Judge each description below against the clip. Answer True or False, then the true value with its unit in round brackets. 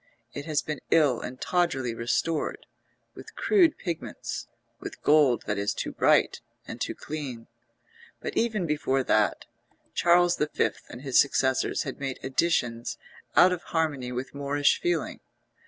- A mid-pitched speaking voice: True (145 Hz)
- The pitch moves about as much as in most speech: True (4.8 semitones)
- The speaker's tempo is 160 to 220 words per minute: False (140 wpm)